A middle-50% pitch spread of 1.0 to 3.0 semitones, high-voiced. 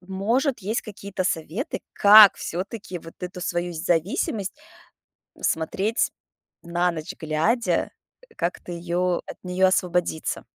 No: average, 2.7 semitones; medium, 180 Hz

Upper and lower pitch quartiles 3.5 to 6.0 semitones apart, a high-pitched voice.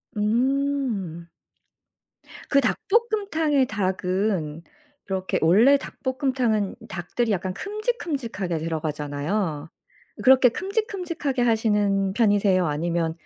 No: wide, 7.4 semitones; high, 215 Hz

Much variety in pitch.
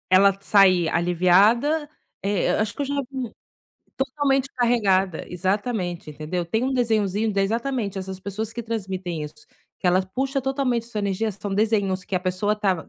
No: average, 4.2 semitones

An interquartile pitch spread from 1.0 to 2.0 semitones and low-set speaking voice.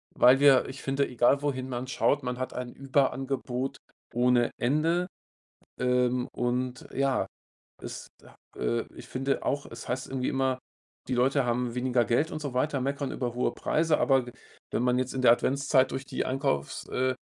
Yes: narrow, 1.7 semitones; low, 130 Hz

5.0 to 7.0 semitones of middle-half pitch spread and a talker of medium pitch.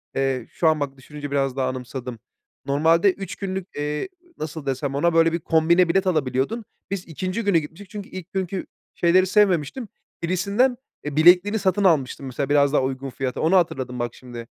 Yes: wide, 5.4 semitones; medium, 160 Hz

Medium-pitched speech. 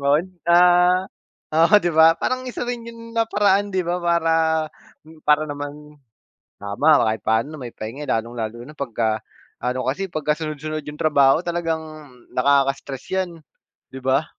Yes: medium, 155 Hz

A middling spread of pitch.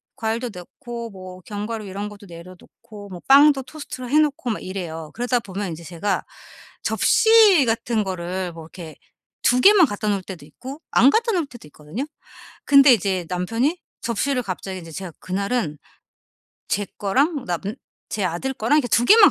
No: wide, 6.2 semitones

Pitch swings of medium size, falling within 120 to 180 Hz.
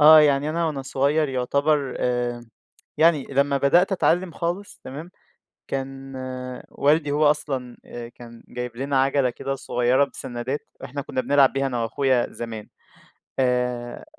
Yes: average, 3.0 semitones; low, 135 Hz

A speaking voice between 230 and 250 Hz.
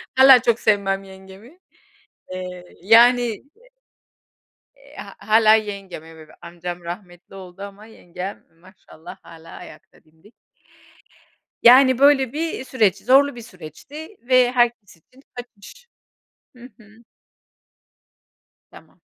No: high, 215 Hz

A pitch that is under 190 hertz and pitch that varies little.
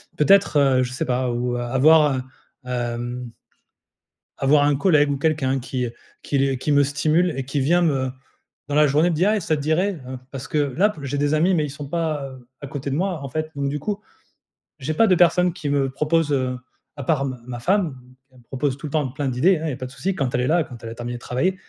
No: medium, 140 Hz; average, 3.4 semitones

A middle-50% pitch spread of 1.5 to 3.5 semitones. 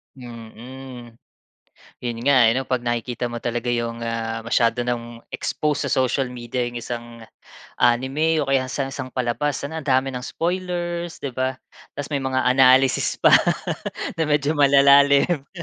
Yes: average, 2.9 semitones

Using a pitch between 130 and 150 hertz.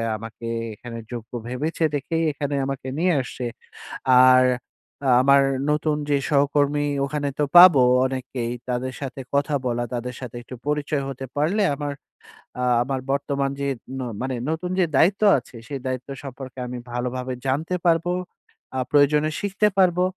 Yes: medium, 140 Hz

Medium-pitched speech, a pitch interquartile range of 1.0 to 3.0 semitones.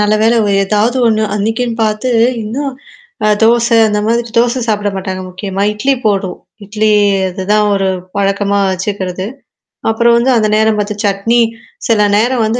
No: high, 215 Hz; narrow, 2.6 semitones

